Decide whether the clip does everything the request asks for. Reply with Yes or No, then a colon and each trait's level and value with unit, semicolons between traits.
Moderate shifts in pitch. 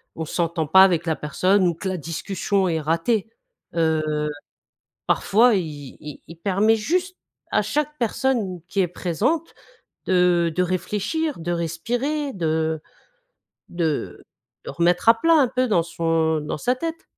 No: wide, 5.8 semitones